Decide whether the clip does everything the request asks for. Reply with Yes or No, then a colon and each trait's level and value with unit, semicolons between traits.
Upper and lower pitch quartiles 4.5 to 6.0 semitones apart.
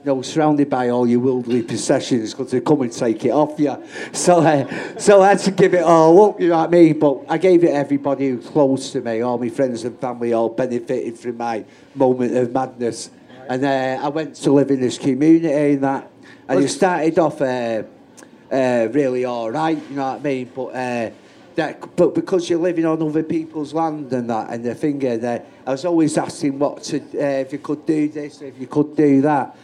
No: average, 3.7 semitones